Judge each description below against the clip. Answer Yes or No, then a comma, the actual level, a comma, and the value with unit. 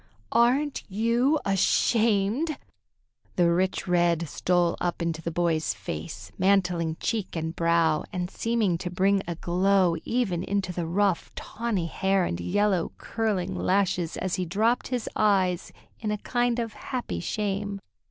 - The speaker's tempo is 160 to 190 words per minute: No, average, 145 wpm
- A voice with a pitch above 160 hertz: Yes, high, 190 Hz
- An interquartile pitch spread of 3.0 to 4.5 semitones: Yes, average, 3.9 semitones